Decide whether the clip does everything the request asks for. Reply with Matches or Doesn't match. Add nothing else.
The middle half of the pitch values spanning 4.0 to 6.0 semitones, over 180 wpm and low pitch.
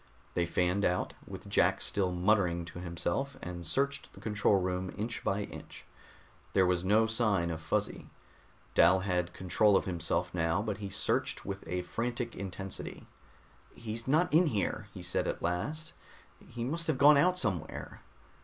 Doesn't match